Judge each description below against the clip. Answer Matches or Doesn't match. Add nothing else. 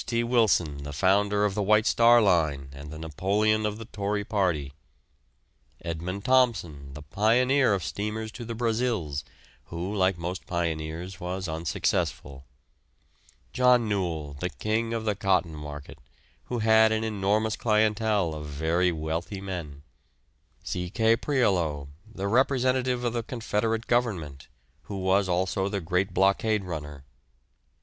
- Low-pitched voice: Matches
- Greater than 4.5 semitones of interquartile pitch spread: Matches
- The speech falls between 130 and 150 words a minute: Matches